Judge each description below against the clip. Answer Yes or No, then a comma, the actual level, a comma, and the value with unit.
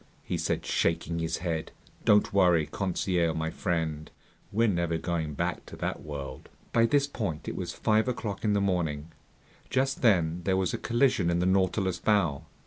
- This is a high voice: No, very low, 90 Hz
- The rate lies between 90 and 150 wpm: No, average, 175 wpm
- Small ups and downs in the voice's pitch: No, average, 4.1 semitones